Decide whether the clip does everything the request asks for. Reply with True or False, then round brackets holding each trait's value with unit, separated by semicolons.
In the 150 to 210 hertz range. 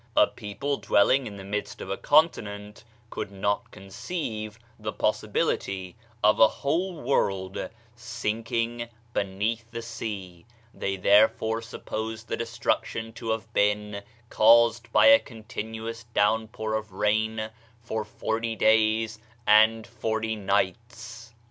False (110 Hz)